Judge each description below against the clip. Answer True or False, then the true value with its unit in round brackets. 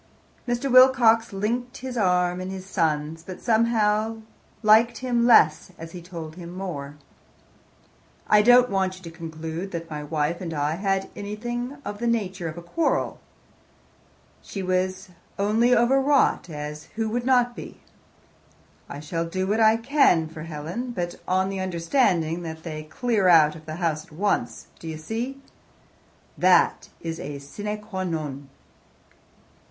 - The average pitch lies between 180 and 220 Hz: True (185 Hz)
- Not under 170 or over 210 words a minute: False (155 wpm)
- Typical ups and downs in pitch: False (5.7 semitones)